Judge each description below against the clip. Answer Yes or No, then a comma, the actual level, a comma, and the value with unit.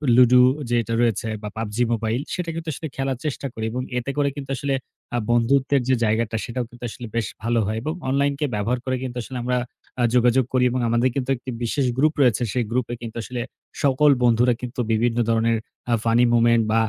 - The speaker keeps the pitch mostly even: Yes, narrow, 2.3 semitones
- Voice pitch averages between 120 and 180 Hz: Yes, low, 125 Hz